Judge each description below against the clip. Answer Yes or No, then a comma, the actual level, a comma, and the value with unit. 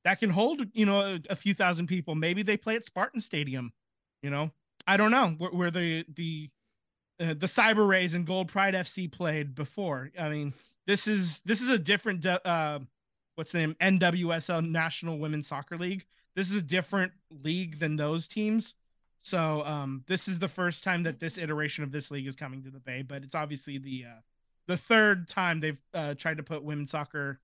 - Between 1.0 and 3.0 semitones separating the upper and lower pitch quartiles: No, average, 4.1 semitones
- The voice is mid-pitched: Yes, medium, 165 Hz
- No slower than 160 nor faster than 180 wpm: No, fast, 205 wpm